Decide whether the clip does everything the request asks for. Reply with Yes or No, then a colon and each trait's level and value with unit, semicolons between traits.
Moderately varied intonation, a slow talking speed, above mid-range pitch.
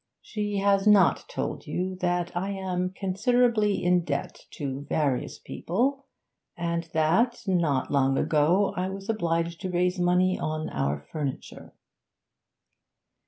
No: average, 3.8 semitones; slow, 125 wpm; medium, 180 Hz